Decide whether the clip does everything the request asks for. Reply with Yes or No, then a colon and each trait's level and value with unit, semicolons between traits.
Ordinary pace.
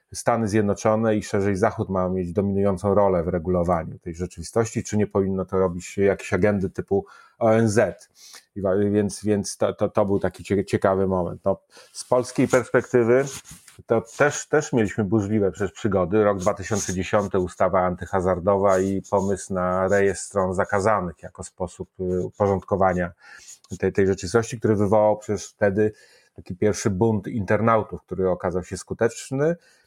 Yes: average, 140 wpm